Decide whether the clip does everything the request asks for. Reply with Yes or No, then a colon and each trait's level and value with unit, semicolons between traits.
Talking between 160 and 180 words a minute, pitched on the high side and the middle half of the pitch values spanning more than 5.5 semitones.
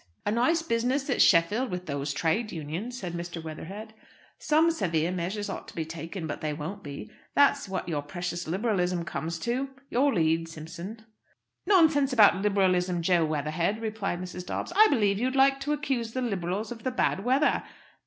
Yes: average, 175 wpm; high, 195 Hz; wide, 6.3 semitones